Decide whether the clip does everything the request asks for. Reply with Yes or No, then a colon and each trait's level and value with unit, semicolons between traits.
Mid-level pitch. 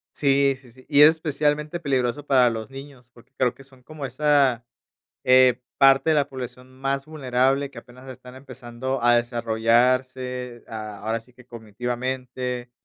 No: low, 130 Hz